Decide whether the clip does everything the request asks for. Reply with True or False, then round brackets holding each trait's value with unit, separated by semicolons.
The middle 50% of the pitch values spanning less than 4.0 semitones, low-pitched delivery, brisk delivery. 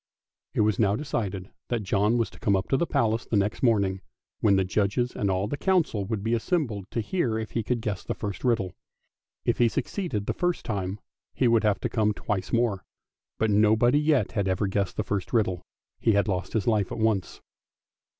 True (3.0 semitones; 105 Hz; 220 wpm)